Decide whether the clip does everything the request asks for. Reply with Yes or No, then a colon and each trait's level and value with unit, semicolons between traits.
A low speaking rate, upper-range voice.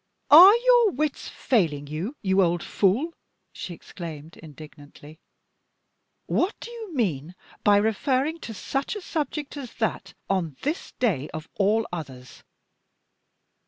Yes: slow, 125 wpm; high, 205 Hz